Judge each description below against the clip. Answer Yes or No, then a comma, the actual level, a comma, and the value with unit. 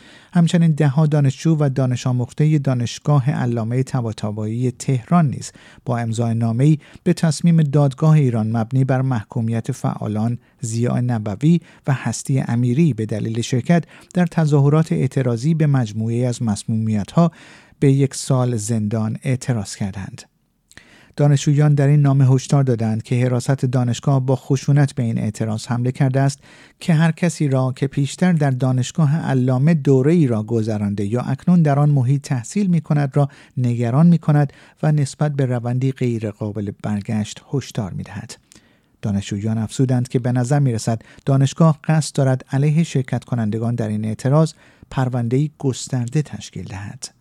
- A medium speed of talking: Yes, average, 145 wpm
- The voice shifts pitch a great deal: No, average, 4.1 semitones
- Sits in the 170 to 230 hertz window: No, low, 130 Hz